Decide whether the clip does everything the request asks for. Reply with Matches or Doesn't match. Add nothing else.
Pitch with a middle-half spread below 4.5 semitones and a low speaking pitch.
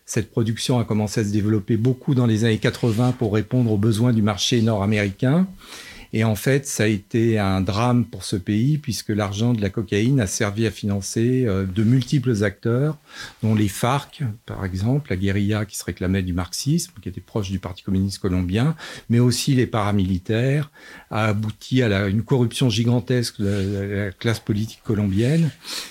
Matches